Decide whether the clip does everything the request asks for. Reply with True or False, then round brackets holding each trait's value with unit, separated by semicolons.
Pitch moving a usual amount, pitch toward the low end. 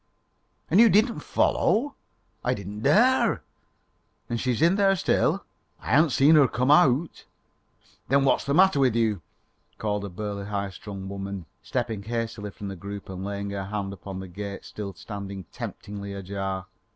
False (5.7 semitones; 105 Hz)